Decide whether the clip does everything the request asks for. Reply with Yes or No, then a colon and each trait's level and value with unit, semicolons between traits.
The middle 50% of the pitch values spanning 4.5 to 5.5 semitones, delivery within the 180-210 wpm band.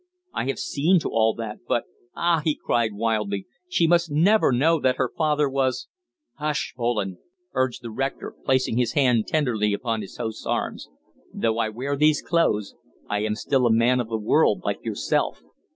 Yes: average, 5.0 semitones; average, 185 wpm